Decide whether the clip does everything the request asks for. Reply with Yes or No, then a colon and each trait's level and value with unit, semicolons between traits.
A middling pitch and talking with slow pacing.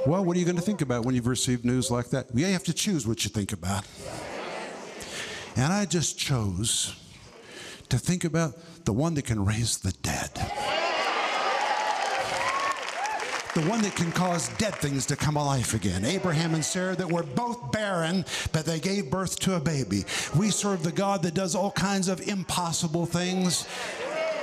No: medium, 165 Hz; average, 175 wpm